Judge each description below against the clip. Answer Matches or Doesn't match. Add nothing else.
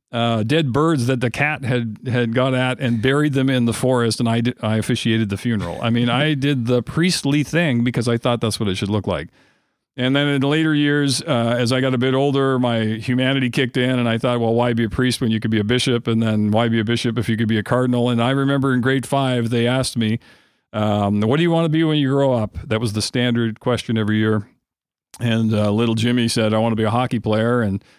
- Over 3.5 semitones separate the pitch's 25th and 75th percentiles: Doesn't match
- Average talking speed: Doesn't match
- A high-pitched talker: Doesn't match